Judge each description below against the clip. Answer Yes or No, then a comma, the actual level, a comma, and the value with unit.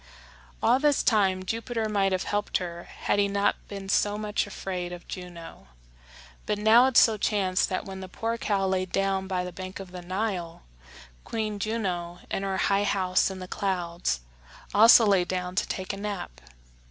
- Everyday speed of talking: Yes, average, 180 wpm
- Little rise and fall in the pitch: Yes, narrow, 2.2 semitones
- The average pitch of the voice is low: No, high, 195 Hz